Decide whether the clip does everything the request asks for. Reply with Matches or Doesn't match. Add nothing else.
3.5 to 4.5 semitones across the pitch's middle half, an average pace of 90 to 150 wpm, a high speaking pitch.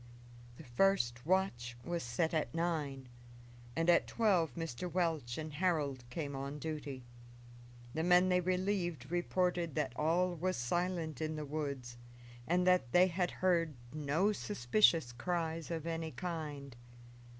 Doesn't match